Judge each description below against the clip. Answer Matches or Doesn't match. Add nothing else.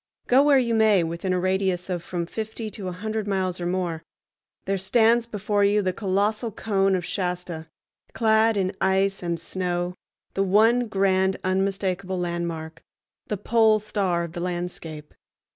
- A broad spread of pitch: Doesn't match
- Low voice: Doesn't match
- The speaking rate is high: Doesn't match